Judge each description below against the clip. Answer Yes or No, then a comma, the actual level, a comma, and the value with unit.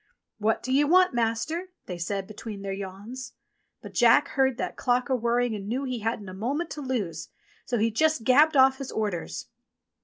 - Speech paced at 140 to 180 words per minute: No, average, 190 wpm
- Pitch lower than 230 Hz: No, high, 235 Hz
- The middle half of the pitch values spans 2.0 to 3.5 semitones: No, average, 4.4 semitones